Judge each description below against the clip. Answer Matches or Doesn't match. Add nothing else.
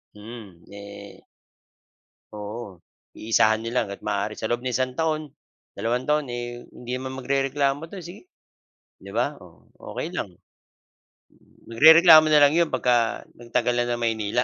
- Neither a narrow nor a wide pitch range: Matches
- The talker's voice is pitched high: Doesn't match